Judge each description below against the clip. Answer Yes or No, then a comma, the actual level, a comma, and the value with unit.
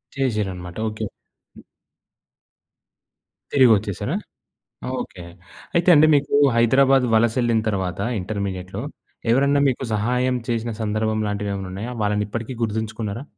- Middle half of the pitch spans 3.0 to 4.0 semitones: Yes, average, 3.6 semitones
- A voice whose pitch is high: No, low, 110 Hz